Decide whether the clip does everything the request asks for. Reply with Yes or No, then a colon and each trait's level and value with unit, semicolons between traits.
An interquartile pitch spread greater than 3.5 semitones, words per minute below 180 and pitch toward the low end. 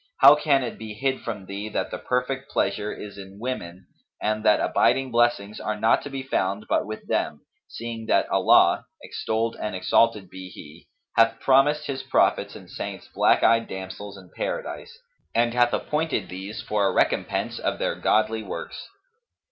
Yes: average, 4.2 semitones; average, 170 wpm; low, 110 Hz